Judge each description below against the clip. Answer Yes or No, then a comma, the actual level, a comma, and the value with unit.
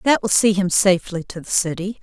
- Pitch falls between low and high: No, high, 195 Hz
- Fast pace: Yes, fast, 235 wpm